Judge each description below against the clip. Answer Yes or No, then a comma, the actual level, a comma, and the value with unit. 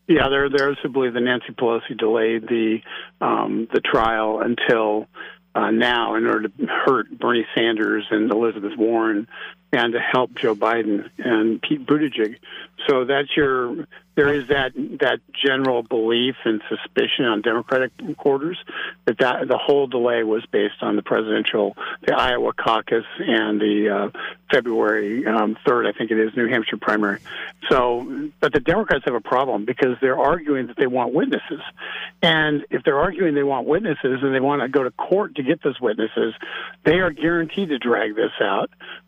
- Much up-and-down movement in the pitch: No, average, 4.3 semitones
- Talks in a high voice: No, low, 120 Hz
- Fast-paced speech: No, average, 170 wpm